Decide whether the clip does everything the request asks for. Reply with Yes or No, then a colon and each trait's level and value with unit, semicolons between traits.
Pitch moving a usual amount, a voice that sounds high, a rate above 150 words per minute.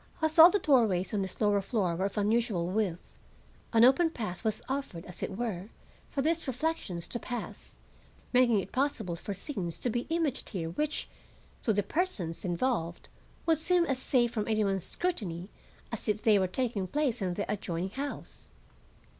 No: wide, 6.1 semitones; high, 220 Hz; average, 180 wpm